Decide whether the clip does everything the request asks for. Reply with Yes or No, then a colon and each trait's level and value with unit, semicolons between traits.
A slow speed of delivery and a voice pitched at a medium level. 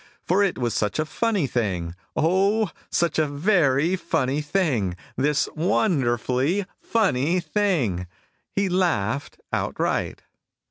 Yes: slow, 110 wpm; medium, 155 Hz